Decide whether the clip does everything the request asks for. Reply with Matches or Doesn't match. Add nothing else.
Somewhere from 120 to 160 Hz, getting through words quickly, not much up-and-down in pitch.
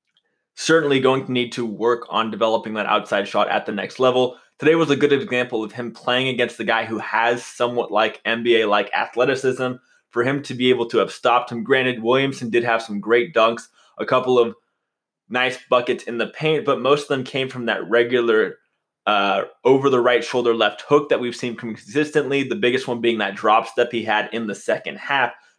Matches